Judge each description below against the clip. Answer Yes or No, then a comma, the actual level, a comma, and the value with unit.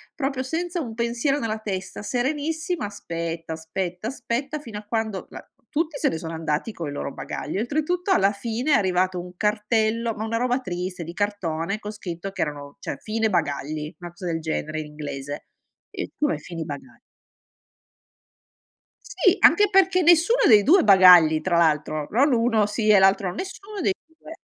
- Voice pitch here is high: Yes, high, 210 Hz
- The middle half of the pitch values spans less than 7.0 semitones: No, wide, 7.4 semitones